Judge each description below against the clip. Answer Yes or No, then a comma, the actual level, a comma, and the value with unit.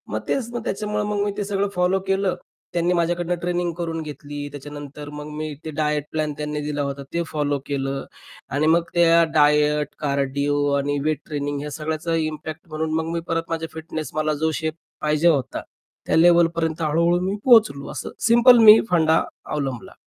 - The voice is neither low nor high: Yes, medium, 155 Hz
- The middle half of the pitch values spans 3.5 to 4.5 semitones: No, average, 2.7 semitones